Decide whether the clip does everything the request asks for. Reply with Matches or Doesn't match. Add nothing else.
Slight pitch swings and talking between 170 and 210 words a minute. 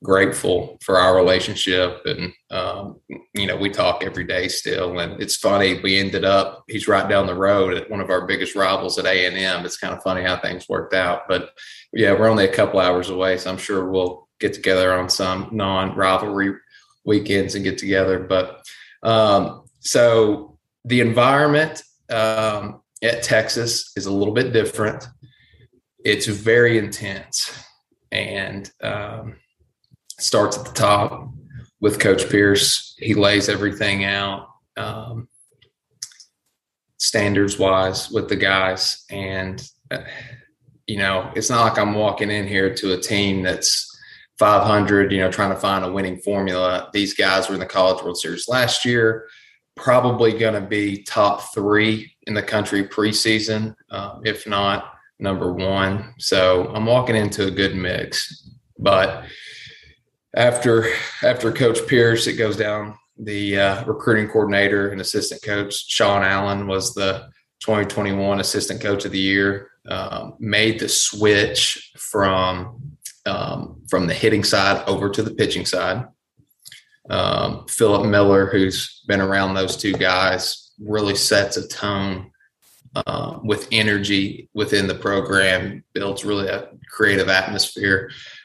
Doesn't match